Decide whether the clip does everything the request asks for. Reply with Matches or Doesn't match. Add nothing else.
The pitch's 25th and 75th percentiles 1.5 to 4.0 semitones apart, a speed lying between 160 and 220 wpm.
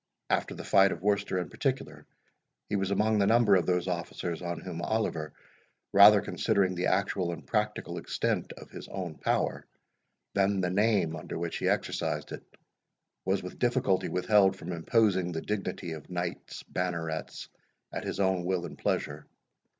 Matches